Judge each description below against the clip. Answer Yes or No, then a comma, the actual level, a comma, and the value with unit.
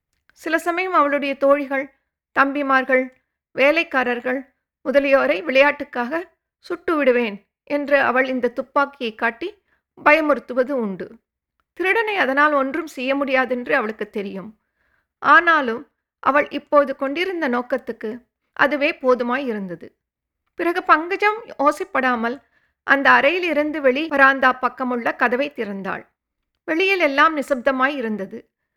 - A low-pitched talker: No, very high, 275 Hz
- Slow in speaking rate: Yes, slow, 100 wpm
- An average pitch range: Yes, average, 3.2 semitones